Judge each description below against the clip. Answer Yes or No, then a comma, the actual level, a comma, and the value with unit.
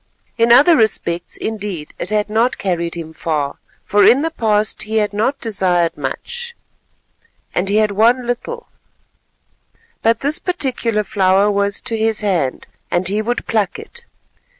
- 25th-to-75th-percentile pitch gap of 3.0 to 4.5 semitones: Yes, average, 4.1 semitones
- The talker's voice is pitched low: No, high, 215 Hz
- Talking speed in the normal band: Yes, average, 150 wpm